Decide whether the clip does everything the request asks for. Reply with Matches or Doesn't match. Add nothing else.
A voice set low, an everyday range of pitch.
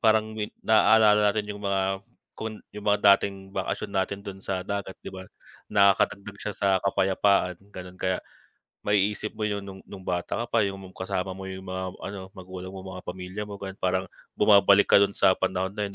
Doesn't match